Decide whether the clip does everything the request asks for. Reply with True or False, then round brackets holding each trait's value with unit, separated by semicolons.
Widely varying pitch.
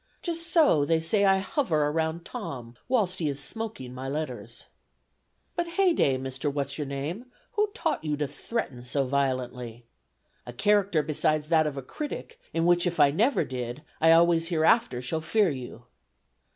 True (6.5 semitones)